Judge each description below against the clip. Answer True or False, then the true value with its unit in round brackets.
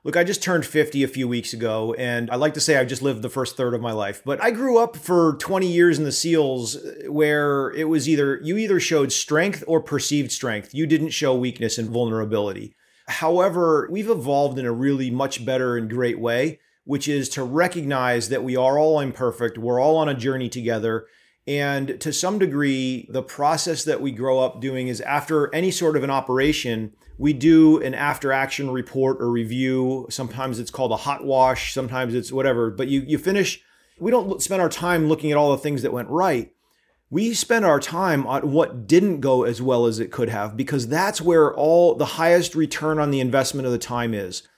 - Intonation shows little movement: False (3.8 semitones)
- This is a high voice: False (140 Hz)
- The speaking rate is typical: False (210 wpm)